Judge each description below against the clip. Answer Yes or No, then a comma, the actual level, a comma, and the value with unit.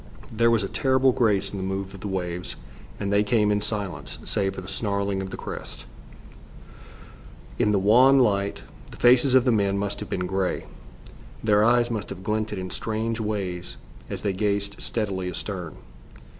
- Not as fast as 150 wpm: No, average, 180 wpm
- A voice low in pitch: Yes, low, 100 Hz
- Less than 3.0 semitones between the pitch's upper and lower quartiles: Yes, narrow, 2.5 semitones